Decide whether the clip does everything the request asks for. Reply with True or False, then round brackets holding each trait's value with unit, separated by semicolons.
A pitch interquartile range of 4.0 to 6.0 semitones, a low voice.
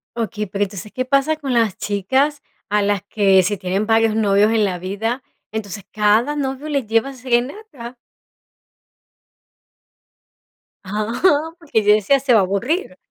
False (4.7 semitones; 220 Hz)